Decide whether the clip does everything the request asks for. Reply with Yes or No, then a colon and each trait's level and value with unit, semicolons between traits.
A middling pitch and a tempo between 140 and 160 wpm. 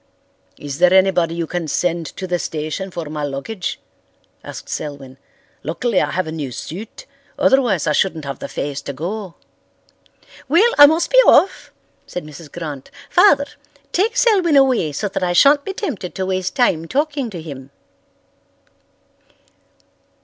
Yes: medium, 180 Hz; average, 155 wpm